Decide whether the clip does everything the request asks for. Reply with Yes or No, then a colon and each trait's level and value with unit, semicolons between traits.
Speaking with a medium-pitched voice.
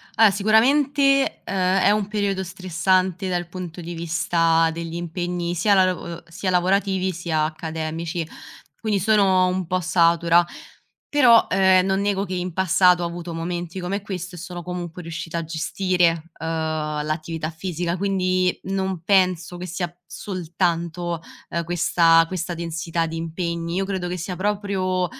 Yes: medium, 180 Hz